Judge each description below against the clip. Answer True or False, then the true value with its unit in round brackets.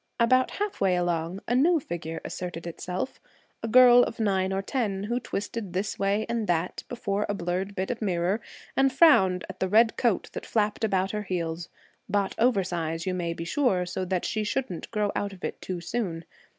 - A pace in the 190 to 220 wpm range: True (195 wpm)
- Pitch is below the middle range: False (195 Hz)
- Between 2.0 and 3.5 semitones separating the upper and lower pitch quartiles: False (4.2 semitones)